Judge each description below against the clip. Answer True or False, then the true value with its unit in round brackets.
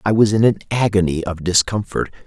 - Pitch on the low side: True (100 Hz)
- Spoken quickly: False (185 wpm)